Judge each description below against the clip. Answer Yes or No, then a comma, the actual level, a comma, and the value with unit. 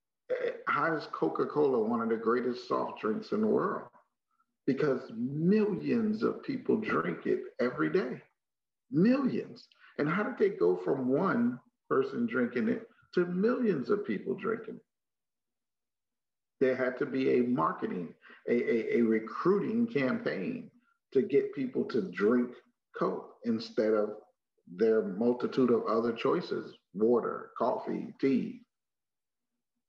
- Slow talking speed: Yes, slow, 130 wpm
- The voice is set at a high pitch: Yes, high, 220 Hz